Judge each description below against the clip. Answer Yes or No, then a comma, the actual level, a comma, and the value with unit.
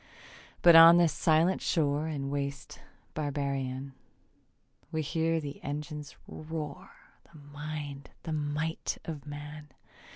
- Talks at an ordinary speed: No, slow, 110 wpm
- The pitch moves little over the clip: Yes, narrow, 1.9 semitones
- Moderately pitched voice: Yes, medium, 150 Hz